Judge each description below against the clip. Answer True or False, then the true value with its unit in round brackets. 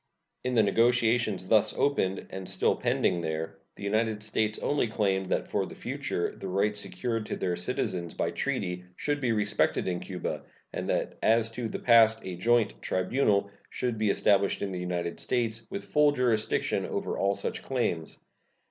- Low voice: True (105 Hz)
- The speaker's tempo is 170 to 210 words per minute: True (175 wpm)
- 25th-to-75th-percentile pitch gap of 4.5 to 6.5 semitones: False (4.0 semitones)